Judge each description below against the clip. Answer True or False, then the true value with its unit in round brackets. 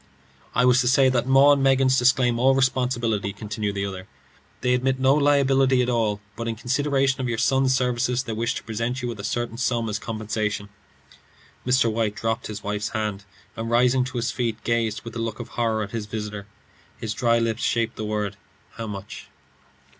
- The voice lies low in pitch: True (115 Hz)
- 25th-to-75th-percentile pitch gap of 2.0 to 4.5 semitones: True (2.9 semitones)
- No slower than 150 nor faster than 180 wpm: False (200 wpm)